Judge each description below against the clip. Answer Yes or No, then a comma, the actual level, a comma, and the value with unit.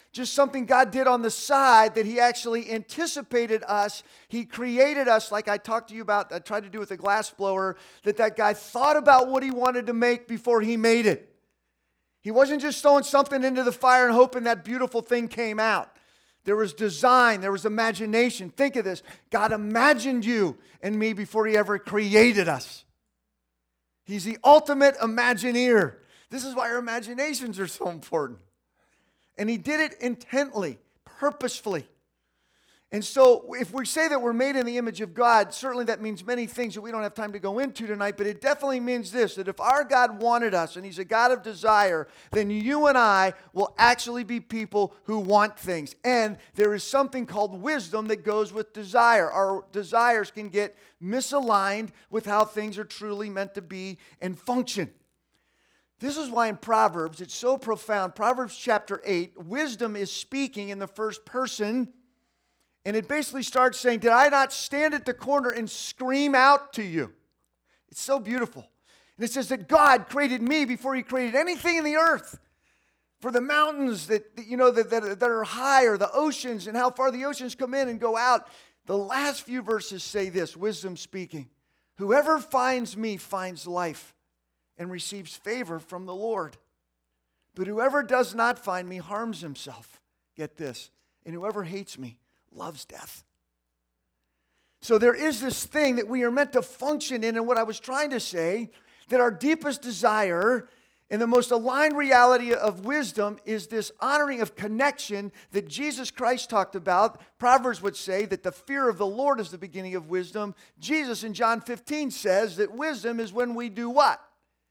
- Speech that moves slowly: No, average, 185 wpm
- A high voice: Yes, high, 230 Hz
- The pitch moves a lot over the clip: No, average, 3.9 semitones